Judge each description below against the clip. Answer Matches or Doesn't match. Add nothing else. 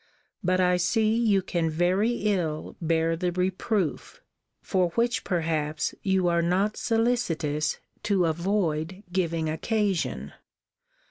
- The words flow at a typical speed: Doesn't match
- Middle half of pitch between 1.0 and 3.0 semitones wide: Doesn't match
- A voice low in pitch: Doesn't match